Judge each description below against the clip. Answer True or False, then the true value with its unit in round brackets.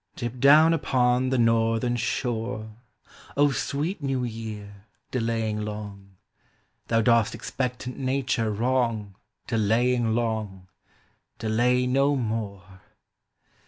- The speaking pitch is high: False (115 Hz)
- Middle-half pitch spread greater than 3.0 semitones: False (2.7 semitones)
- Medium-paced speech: False (95 wpm)